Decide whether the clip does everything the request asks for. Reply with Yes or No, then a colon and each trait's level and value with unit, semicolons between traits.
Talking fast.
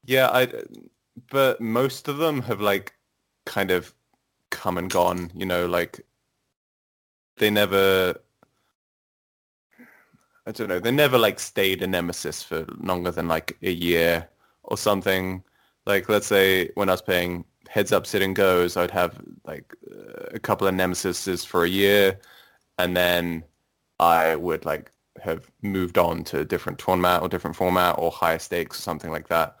No: average, 160 wpm